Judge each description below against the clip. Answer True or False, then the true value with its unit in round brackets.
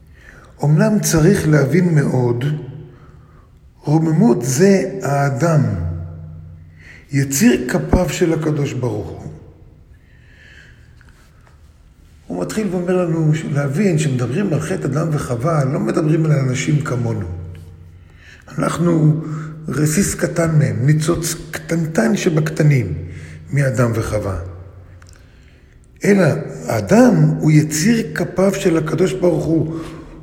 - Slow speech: True (90 wpm)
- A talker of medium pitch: True (150 Hz)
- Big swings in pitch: True (8.9 semitones)